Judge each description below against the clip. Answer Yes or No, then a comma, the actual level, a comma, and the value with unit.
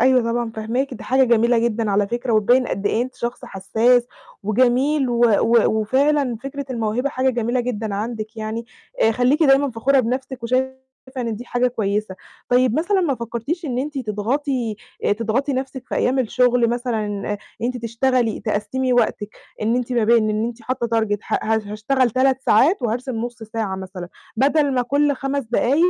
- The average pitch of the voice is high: Yes, high, 240 Hz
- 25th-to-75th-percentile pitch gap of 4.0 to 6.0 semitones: No, average, 3.0 semitones